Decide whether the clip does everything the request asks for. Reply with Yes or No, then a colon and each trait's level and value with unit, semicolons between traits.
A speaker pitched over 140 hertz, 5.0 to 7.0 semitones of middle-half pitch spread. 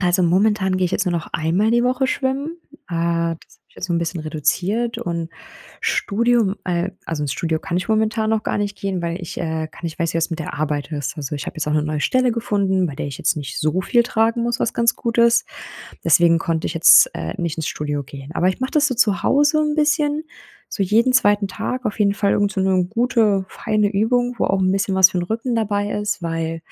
Yes: high, 190 Hz; wide, 5.4 semitones